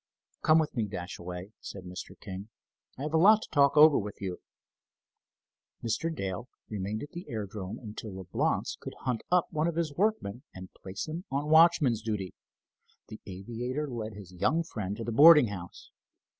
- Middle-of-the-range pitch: No, low, 115 Hz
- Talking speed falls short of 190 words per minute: Yes, average, 170 wpm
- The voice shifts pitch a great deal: Yes, wide, 7.8 semitones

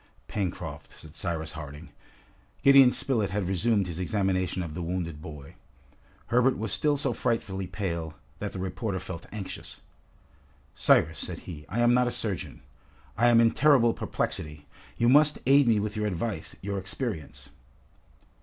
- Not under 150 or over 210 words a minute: Yes, average, 155 wpm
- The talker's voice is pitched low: Yes, low, 100 Hz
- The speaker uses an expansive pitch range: Yes, wide, 5.8 semitones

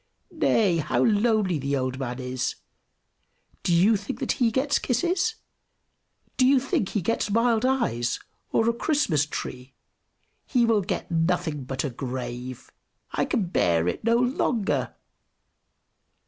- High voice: Yes, high, 195 Hz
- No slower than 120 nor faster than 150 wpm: Yes, average, 140 wpm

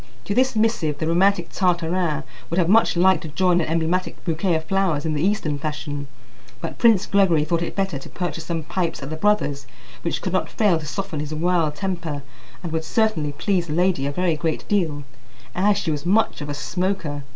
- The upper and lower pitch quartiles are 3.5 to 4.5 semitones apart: Yes, average, 3.9 semitones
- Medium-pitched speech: Yes, medium, 170 Hz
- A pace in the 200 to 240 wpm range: Yes, fast, 205 wpm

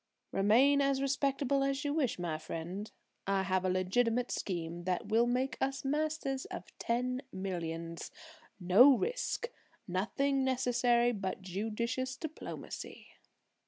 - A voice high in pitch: Yes, high, 240 Hz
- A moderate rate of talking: No, slow, 125 wpm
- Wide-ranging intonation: Yes, wide, 6.3 semitones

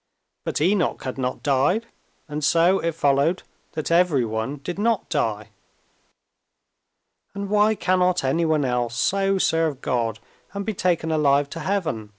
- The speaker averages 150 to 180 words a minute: No, average, 140 wpm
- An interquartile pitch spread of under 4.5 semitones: No, wide, 5.5 semitones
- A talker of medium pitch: Yes, medium, 160 Hz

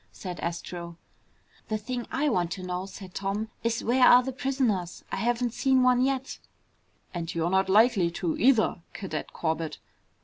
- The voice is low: No, high, 205 Hz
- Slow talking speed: No, average, 165 wpm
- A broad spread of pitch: Yes, wide, 5.8 semitones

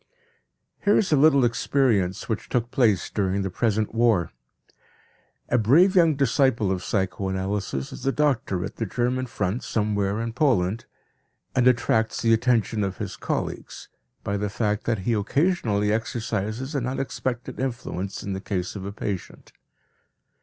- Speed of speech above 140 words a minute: Yes, average, 150 wpm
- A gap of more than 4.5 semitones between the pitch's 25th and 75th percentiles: No, average, 4.1 semitones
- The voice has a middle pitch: No, low, 110 Hz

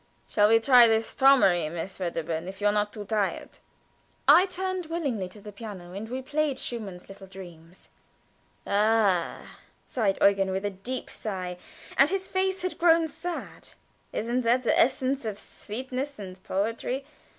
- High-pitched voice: Yes, high, 220 Hz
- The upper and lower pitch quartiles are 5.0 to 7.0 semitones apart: Yes, wide, 5.6 semitones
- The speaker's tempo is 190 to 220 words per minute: No, average, 160 wpm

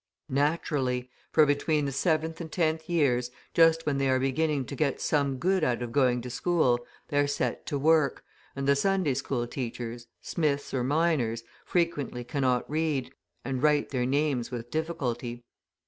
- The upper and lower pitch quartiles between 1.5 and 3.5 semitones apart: No, average, 3.9 semitones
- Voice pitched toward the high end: No, medium, 140 Hz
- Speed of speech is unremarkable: Yes, average, 165 wpm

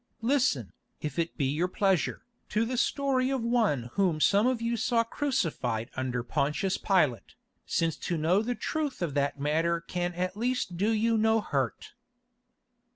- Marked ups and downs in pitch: Yes, wide, 7.3 semitones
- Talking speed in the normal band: Yes, average, 160 wpm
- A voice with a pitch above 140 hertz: Yes, medium, 185 Hz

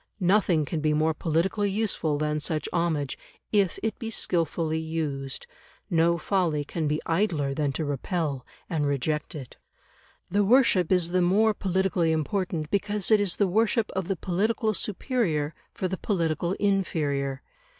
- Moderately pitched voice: Yes, medium, 170 Hz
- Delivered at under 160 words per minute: Yes, average, 150 wpm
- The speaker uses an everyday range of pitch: Yes, average, 4.4 semitones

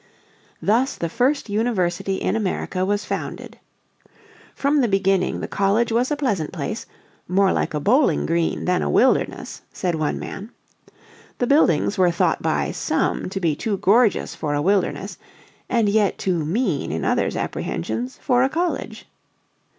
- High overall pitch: Yes, high, 195 Hz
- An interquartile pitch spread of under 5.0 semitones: No, wide, 5.5 semitones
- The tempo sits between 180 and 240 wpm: No, average, 155 wpm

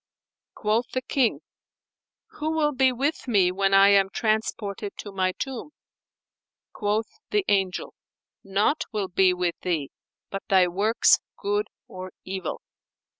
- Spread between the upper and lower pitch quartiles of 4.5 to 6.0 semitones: Yes, average, 4.9 semitones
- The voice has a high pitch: Yes, high, 205 Hz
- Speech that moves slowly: Yes, slow, 130 wpm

